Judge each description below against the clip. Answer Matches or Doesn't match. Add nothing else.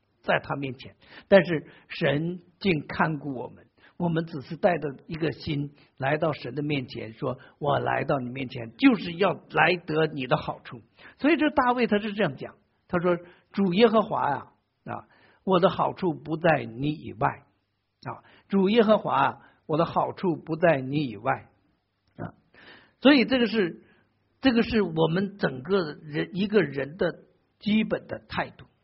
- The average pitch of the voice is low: Doesn't match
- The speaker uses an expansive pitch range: Matches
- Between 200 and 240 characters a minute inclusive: Matches